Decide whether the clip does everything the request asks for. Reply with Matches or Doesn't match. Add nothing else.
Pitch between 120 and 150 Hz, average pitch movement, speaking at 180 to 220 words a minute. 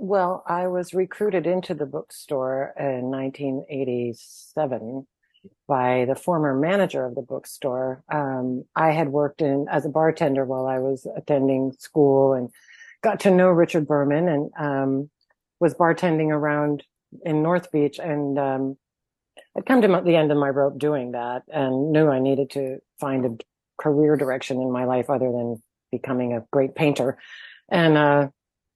Doesn't match